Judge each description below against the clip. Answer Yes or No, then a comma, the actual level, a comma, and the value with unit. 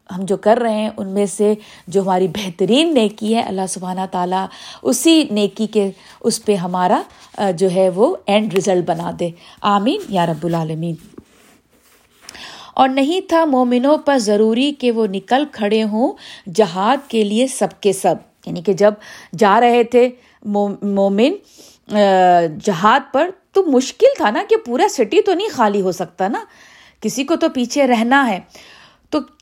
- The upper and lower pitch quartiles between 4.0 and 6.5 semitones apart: Yes, wide, 5.5 semitones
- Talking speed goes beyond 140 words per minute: Yes, average, 160 wpm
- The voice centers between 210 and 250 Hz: Yes, high, 215 Hz